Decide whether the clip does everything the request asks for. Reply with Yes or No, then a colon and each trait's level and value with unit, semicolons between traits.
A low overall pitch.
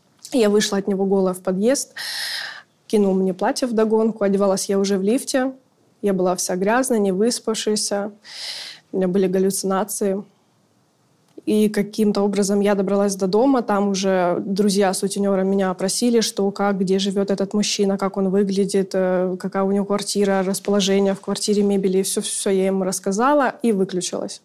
No: high, 200 Hz